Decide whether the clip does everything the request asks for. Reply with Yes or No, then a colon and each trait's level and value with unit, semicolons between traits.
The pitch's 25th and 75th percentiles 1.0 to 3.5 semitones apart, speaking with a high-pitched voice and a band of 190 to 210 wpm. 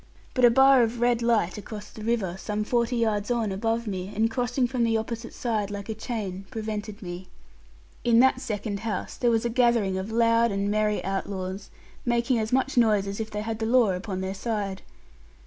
Yes: average, 2.7 semitones; high, 220 Hz; average, 200 wpm